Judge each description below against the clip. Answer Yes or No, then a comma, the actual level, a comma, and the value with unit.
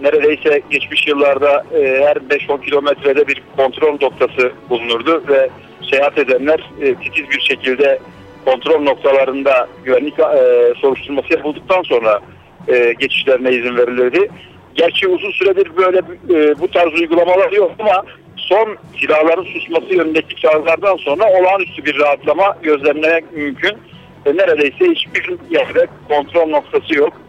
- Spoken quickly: No, average, 125 wpm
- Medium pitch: Yes, medium, 155 Hz